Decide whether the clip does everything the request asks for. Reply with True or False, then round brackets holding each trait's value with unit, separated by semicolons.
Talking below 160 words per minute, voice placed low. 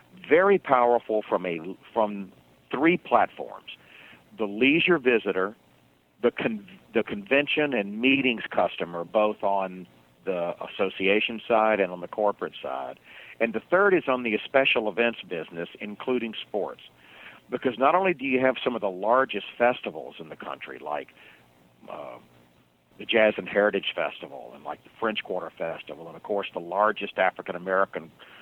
True (150 wpm; 105 Hz)